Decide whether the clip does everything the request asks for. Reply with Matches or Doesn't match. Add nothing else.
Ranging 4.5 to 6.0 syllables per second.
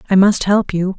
Matches